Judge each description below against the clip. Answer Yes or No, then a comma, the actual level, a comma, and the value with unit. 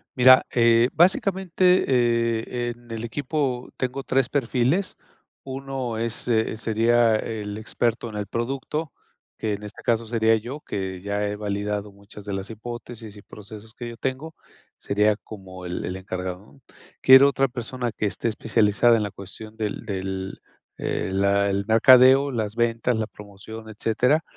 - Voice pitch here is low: Yes, low, 115 Hz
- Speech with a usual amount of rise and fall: Yes, average, 3.4 semitones